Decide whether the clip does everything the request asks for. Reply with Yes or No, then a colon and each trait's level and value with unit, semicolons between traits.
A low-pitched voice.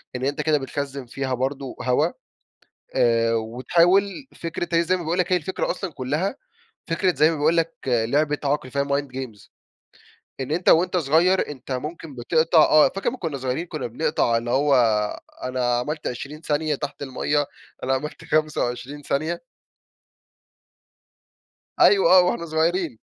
No: medium, 150 Hz